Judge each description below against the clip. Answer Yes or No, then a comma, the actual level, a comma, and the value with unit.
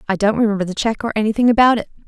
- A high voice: Yes, high, 215 Hz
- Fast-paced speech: Yes, fast, 260 wpm